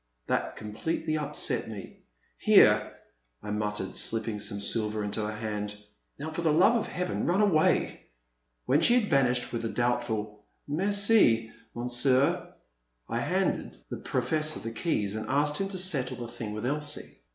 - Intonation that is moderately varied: No, wide, 6.4 semitones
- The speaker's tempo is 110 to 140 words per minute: No, average, 165 wpm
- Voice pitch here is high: No, low, 120 Hz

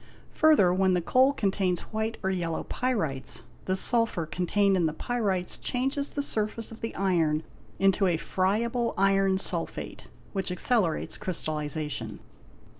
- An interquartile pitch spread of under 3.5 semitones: No, average, 4.6 semitones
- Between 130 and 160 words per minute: Yes, average, 140 wpm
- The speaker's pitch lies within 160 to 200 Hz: Yes, high, 190 Hz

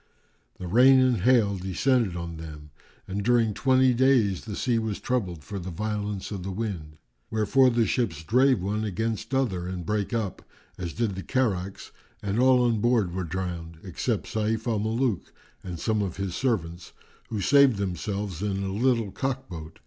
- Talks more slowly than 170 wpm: No, average, 175 wpm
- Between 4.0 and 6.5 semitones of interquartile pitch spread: Yes, average, 4.5 semitones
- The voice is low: Yes, low, 105 Hz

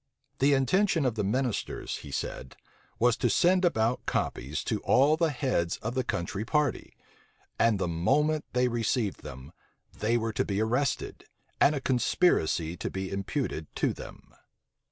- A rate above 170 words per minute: No, average, 155 wpm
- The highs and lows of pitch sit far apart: Yes, wide, 6.3 semitones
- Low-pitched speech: Yes, low, 120 Hz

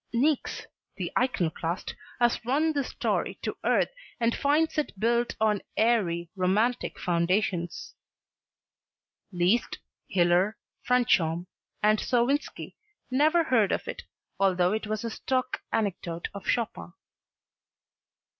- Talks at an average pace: No, slow, 110 wpm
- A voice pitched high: Yes, high, 220 Hz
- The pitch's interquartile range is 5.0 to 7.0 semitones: Yes, wide, 5.6 semitones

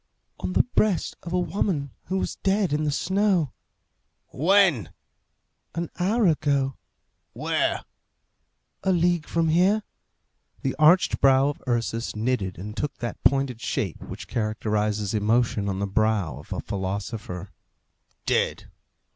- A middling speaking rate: No, slow, 130 wpm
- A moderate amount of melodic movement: No, wide, 8.4 semitones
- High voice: No, low, 135 Hz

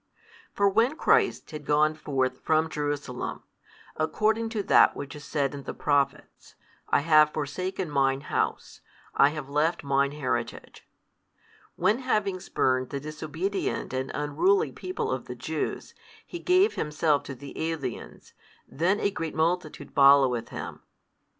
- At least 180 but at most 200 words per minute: No, average, 140 wpm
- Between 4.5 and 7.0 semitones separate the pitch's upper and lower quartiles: Yes, average, 5.0 semitones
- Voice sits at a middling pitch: Yes, medium, 150 Hz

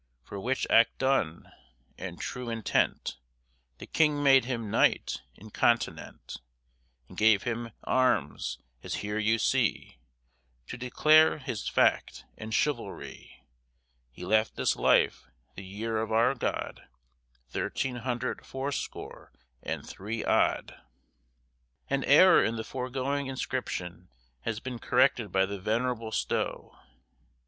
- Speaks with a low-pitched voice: Yes, low, 115 Hz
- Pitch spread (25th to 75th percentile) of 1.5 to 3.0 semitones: No, average, 3.6 semitones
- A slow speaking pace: Yes, slow, 120 wpm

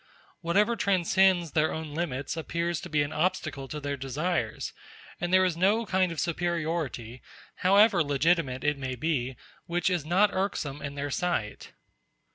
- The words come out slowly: No, average, 155 wpm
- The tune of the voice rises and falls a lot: No, average, 4.1 semitones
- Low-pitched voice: No, medium, 165 Hz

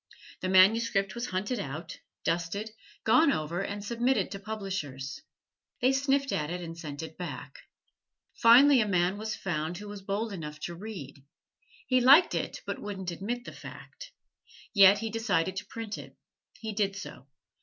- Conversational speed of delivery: Yes, average, 165 wpm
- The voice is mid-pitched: No, high, 200 Hz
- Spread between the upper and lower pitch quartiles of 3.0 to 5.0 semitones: Yes, average, 4.6 semitones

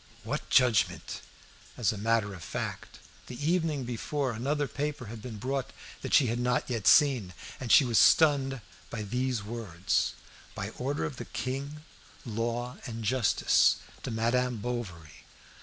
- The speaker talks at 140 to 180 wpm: Yes, average, 150 wpm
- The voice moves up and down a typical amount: Yes, average, 3.2 semitones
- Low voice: Yes, low, 125 Hz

